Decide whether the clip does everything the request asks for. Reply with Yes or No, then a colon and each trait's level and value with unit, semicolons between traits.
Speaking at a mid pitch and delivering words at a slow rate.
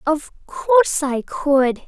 No: very high, 305 Hz; slow, 130 wpm